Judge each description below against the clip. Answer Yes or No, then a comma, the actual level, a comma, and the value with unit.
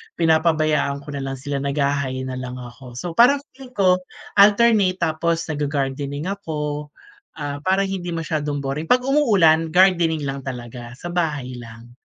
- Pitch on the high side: No, medium, 150 Hz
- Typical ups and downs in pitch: Yes, average, 4.5 semitones